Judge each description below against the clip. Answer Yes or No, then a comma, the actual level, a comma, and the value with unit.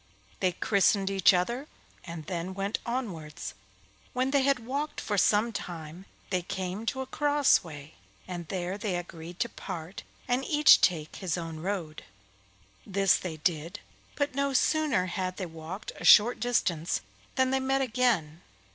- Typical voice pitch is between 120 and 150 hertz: No, high, 195 Hz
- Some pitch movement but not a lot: No, wide, 6.5 semitones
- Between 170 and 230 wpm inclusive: No, average, 155 wpm